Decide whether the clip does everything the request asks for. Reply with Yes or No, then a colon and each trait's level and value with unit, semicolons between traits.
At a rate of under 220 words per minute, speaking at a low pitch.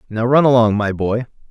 Yes: average, 200 wpm; low, 115 Hz